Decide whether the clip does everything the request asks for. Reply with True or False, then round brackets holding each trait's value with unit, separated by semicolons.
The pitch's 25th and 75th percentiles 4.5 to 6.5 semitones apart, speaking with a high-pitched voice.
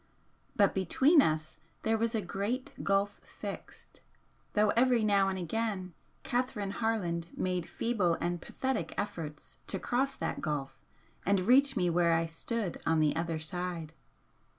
True (5.2 semitones; 195 Hz)